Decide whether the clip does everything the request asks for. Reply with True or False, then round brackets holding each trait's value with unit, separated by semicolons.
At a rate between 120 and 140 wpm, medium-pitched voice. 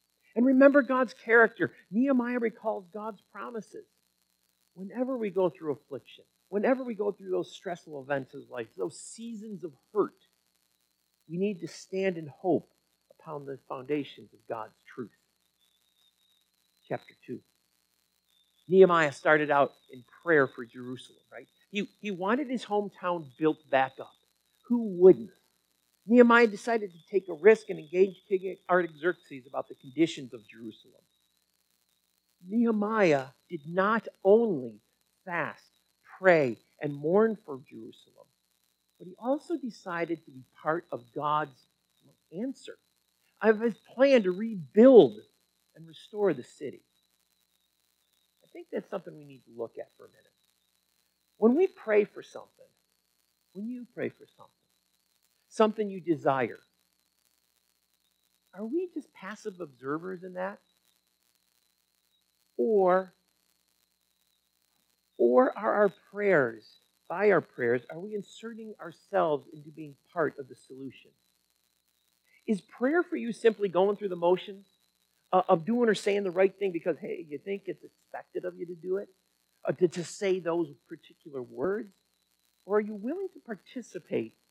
True (135 wpm; 170 Hz)